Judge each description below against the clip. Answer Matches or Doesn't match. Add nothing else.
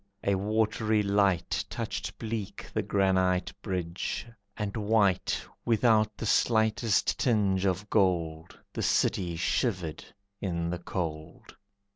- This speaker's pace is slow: Matches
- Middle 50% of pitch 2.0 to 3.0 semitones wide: Doesn't match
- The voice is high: Doesn't match